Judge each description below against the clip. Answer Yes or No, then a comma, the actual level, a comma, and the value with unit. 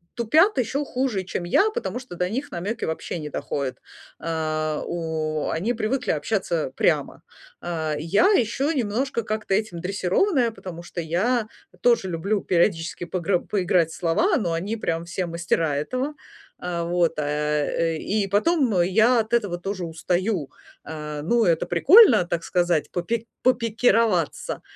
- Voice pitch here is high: No, medium, 180 Hz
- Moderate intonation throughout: No, wide, 5.7 semitones